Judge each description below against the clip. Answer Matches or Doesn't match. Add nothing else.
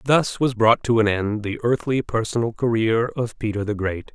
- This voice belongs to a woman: Doesn't match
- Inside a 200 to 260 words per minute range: Matches